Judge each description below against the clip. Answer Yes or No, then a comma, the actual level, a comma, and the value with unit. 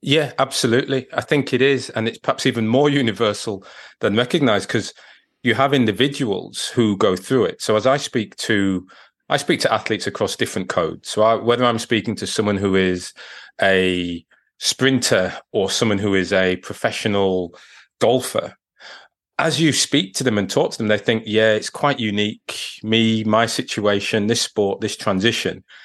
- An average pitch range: Yes, average, 3.8 semitones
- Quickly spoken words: No, average, 170 wpm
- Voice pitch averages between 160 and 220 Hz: No, low, 110 Hz